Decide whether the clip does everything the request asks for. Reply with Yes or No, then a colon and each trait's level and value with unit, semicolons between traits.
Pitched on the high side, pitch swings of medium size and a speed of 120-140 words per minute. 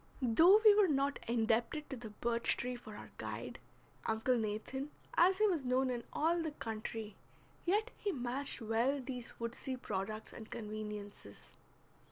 No: high, 245 Hz; average, 4.4 semitones; average, 155 wpm